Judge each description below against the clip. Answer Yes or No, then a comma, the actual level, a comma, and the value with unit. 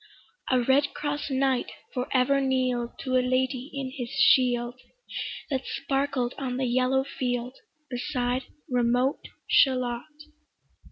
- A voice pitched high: Yes, very high, 255 Hz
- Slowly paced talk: Yes, slow, 115 wpm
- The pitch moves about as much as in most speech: No, narrow, 1.5 semitones